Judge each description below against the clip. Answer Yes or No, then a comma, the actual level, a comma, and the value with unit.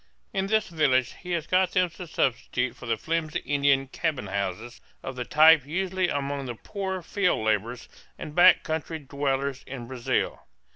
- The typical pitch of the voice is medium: Yes, medium, 145 Hz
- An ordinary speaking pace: Yes, average, 165 wpm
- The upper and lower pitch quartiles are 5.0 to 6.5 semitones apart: Yes, wide, 5.5 semitones